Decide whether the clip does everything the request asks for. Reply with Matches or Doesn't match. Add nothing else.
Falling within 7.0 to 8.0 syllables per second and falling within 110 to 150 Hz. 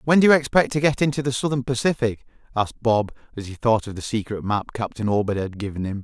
Doesn't match